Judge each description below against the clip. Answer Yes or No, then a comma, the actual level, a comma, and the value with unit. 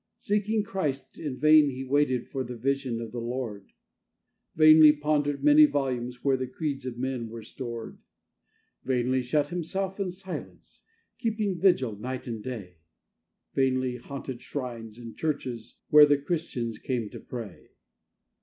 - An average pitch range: Yes, average, 4.0 semitones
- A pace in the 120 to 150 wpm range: Yes, average, 145 wpm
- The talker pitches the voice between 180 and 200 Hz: No, low, 130 Hz